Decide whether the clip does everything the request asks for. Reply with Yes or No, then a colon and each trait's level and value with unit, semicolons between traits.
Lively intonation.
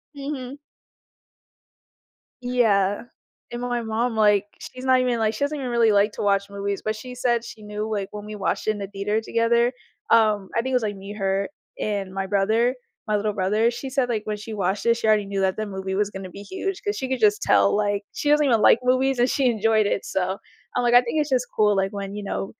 No: average, 3.4 semitones